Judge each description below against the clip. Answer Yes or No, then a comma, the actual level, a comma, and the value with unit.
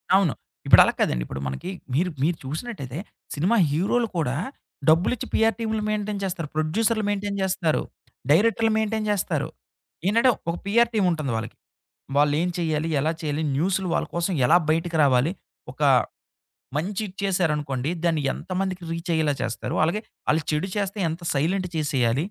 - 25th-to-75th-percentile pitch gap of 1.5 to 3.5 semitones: No, average, 4.9 semitones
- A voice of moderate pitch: Yes, medium, 175 Hz